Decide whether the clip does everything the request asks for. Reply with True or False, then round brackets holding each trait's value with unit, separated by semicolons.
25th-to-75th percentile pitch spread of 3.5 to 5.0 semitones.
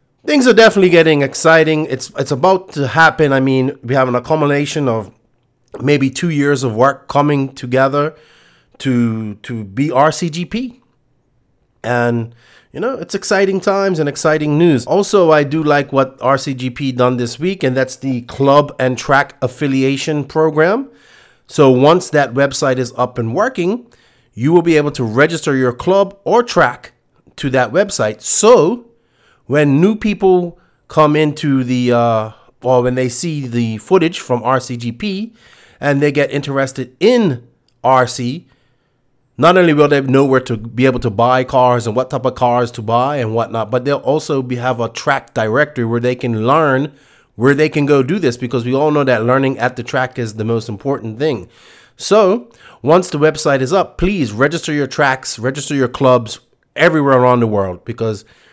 True (3.9 semitones)